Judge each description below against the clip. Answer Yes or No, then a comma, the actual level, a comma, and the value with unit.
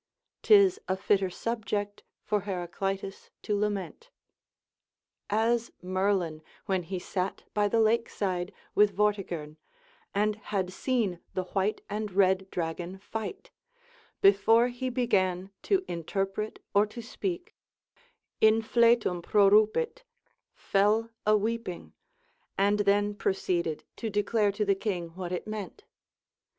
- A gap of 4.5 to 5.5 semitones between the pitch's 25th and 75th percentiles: No, average, 2.8 semitones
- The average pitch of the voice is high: Yes, high, 205 Hz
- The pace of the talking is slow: Yes, slow, 120 wpm